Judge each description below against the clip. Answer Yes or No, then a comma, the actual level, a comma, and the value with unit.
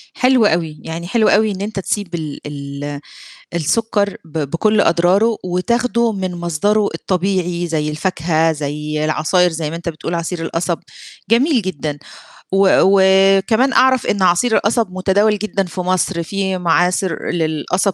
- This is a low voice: No, medium, 180 Hz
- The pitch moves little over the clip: No, average, 3.9 semitones